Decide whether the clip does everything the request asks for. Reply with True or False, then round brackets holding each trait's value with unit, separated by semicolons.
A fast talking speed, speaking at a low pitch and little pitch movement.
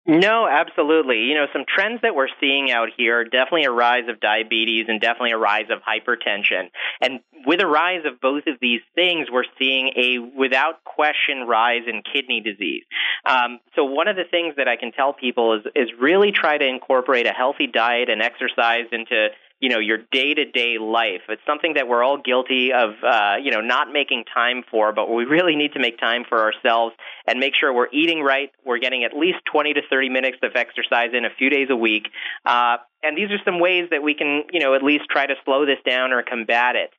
False (220 wpm; 130 Hz; 4.1 semitones)